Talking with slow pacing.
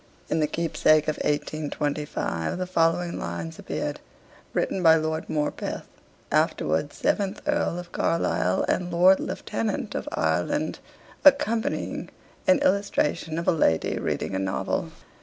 Yes: slow, 125 wpm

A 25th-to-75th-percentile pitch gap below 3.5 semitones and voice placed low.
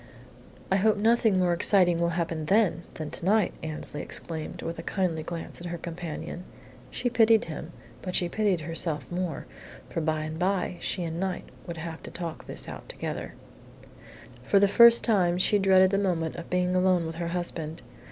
No: average, 2.7 semitones; medium, 175 Hz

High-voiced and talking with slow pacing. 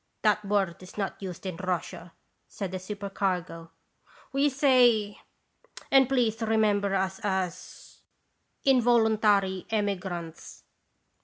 Yes: high, 200 Hz; slow, 110 wpm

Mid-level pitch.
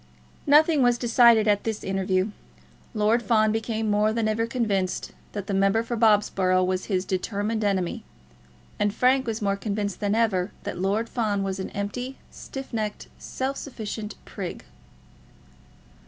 No: high, 215 Hz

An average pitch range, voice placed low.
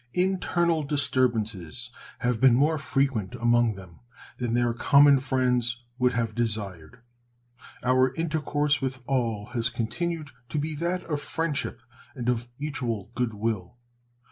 Yes: average, 3.9 semitones; low, 125 Hz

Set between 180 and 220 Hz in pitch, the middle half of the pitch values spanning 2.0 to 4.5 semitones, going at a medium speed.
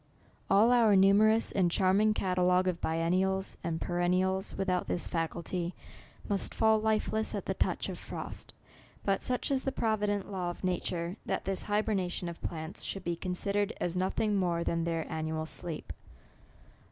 Yes: medium, 185 Hz; average, 2.9 semitones; average, 165 wpm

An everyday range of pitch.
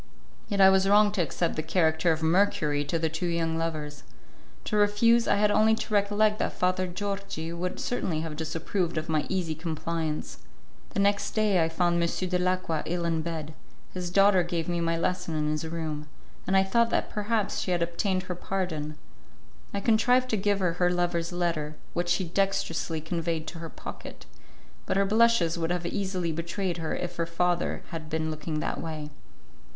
Yes: average, 3.2 semitones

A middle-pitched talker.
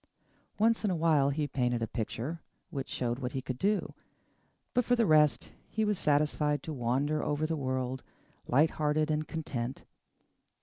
Yes: medium, 150 Hz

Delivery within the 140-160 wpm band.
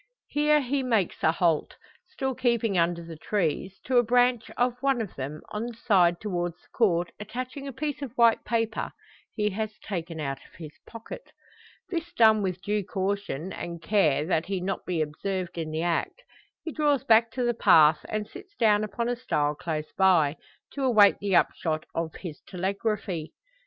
No: average, 185 wpm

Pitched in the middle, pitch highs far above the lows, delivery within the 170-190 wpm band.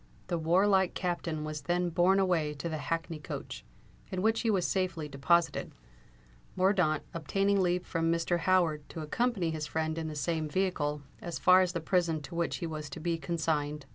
No: medium, 170 Hz; average, 2.8 semitones; average, 185 wpm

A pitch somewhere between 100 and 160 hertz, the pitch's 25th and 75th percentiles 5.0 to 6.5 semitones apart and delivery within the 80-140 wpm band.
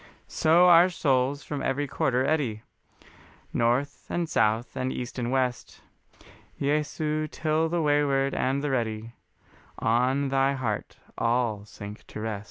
No: low, 135 Hz; average, 3.8 semitones; slow, 135 wpm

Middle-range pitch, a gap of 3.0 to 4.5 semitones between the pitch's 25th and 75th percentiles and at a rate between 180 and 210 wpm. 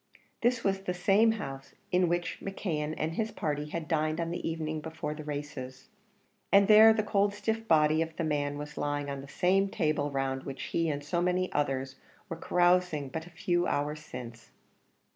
Yes: medium, 160 Hz; average, 3.8 semitones; average, 190 wpm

